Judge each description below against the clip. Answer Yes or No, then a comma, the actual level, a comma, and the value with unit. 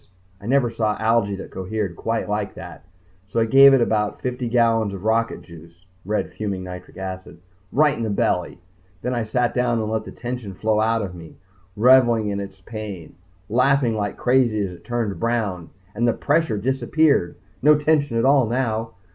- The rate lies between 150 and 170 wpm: No, average, 185 wpm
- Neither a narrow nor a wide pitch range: Yes, average, 3.6 semitones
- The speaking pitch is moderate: No, low, 110 Hz